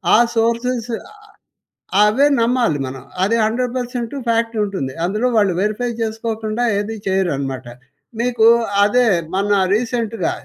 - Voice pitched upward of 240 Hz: No, high, 225 Hz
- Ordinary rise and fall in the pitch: Yes, average, 3.0 semitones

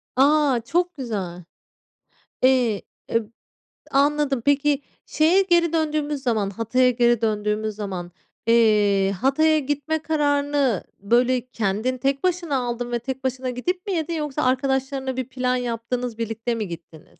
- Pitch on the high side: Yes, very high, 255 Hz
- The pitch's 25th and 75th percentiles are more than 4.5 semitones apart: No, average, 4.1 semitones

